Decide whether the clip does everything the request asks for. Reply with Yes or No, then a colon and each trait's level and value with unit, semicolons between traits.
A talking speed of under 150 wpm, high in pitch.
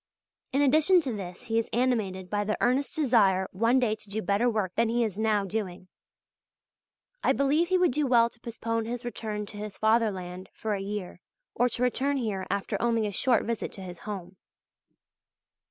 No: average, 190 wpm; high, 220 Hz